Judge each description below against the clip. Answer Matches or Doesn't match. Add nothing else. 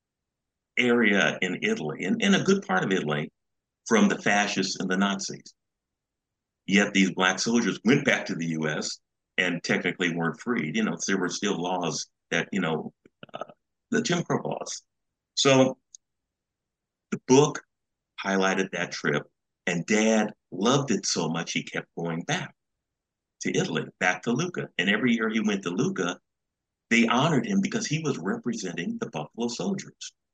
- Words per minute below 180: Matches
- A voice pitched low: Matches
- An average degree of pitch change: Doesn't match